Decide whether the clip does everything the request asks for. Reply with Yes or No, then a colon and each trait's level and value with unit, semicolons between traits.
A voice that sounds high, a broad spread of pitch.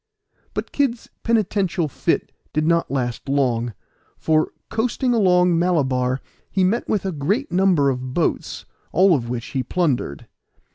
No: medium, 165 Hz; wide, 6.6 semitones